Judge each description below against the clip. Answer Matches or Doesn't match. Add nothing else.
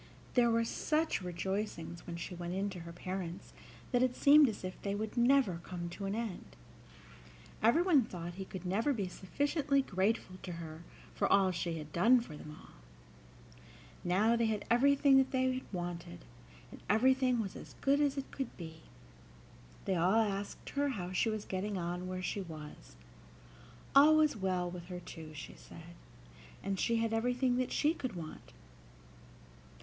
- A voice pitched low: Doesn't match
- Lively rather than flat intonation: Matches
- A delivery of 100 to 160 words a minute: Doesn't match